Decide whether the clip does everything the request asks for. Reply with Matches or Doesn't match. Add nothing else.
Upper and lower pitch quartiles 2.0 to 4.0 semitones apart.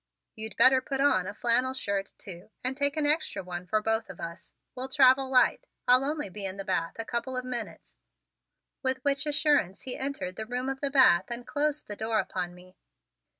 Doesn't match